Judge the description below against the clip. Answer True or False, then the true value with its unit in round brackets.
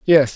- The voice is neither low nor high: True (150 Hz)